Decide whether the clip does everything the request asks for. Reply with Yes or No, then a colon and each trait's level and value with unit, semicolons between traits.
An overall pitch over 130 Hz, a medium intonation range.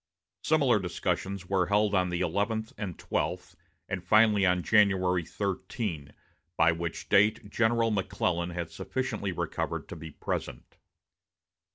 No: very low, 95 Hz; average, 3.3 semitones